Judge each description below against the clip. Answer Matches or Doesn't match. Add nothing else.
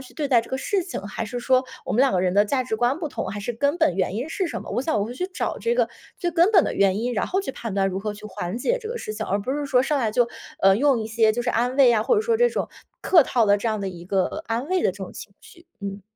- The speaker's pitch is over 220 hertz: Matches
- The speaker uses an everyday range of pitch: Doesn't match